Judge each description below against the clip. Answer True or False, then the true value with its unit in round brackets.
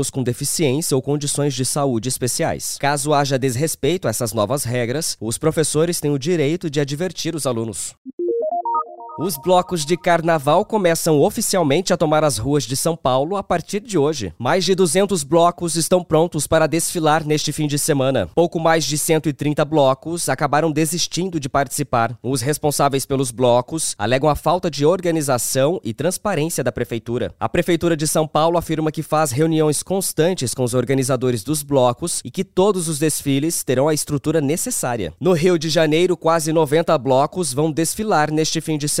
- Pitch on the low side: False (155 Hz)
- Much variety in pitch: False (3.6 semitones)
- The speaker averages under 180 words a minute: True (170 wpm)